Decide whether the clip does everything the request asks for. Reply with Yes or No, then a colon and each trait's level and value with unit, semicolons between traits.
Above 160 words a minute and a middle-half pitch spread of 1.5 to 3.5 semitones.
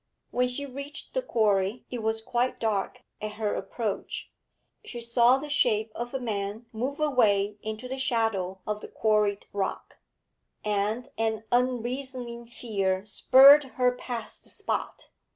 No: average, 145 wpm; average, 3.1 semitones